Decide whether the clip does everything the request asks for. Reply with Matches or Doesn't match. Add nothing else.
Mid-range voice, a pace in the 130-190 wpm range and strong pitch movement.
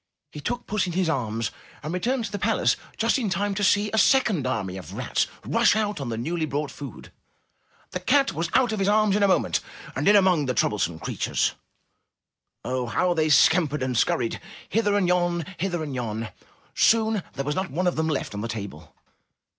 Doesn't match